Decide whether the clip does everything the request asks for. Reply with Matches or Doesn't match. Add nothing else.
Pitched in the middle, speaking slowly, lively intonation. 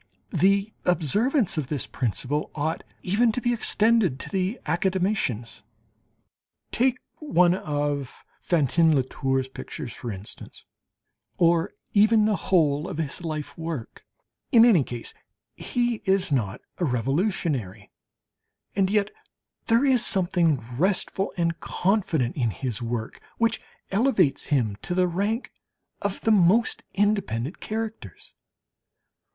Matches